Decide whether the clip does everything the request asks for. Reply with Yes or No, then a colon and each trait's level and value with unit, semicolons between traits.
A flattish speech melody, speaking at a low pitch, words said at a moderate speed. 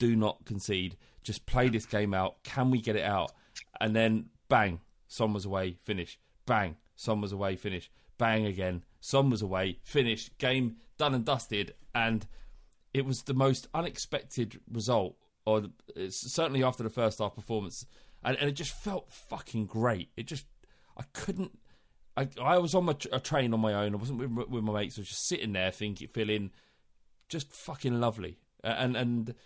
No: average, 4.0 semitones; low, 115 Hz; average, 180 wpm